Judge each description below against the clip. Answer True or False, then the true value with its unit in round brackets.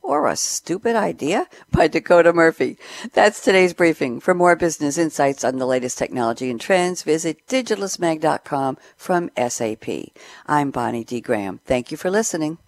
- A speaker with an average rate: True (150 wpm)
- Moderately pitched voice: True (160 Hz)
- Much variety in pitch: True (5.7 semitones)